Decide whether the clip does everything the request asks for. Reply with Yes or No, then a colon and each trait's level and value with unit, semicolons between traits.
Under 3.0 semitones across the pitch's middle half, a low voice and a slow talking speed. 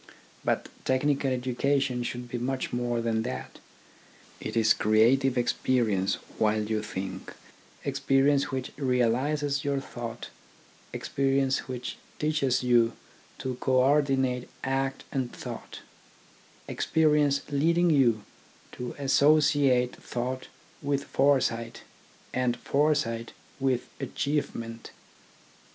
Yes: narrow, 2.6 semitones; low, 130 Hz; slow, 105 wpm